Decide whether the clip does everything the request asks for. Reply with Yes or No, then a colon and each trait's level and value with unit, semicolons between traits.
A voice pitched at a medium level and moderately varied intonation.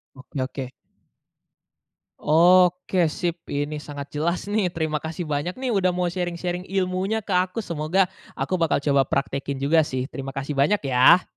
Yes: medium, 165 Hz; average, 4.3 semitones